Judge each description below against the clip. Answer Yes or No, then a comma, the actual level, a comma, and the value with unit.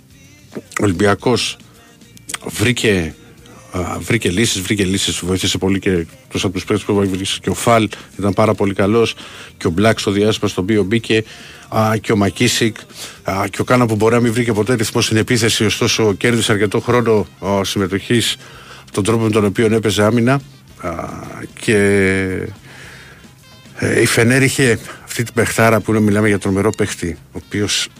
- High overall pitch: No, low, 110 Hz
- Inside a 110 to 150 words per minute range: No, average, 160 wpm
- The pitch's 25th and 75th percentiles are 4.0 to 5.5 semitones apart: No, average, 2.7 semitones